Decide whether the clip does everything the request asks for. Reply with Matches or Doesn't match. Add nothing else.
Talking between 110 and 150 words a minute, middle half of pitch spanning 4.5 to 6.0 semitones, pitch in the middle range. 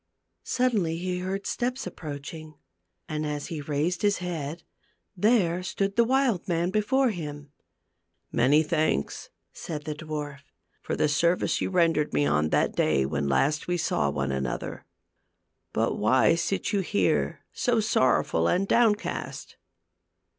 Matches